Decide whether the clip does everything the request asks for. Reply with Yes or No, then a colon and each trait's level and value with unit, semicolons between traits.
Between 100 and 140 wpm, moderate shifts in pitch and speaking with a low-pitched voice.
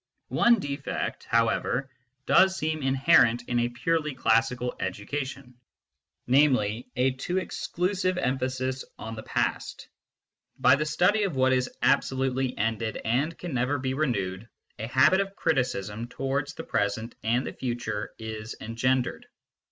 Yes: slow, 135 wpm; average, 3.7 semitones; low, 130 Hz